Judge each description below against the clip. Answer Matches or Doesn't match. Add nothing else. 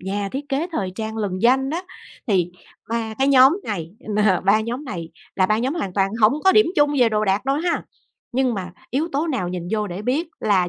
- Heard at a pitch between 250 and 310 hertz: Doesn't match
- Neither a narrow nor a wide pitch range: Doesn't match